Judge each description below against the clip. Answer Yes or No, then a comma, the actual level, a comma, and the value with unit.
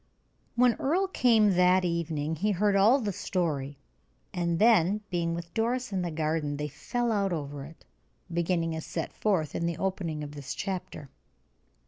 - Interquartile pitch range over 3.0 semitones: Yes, average, 4.6 semitones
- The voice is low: No, medium, 175 Hz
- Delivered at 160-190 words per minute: Yes, average, 165 wpm